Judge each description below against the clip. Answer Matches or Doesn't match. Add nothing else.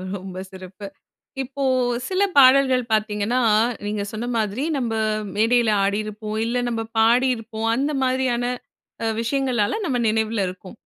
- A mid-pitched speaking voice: Doesn't match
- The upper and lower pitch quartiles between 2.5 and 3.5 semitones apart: Matches